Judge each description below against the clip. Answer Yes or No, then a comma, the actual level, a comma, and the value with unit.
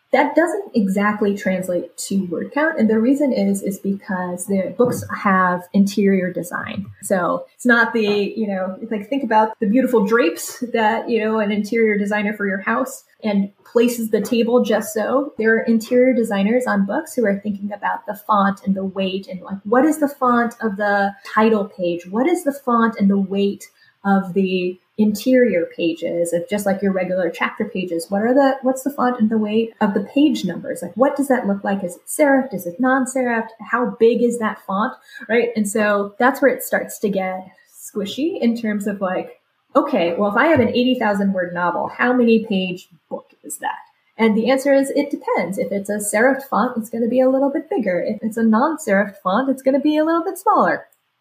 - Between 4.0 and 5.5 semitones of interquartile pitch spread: Yes, average, 4.6 semitones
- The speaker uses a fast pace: Yes, fast, 210 wpm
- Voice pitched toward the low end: No, high, 220 Hz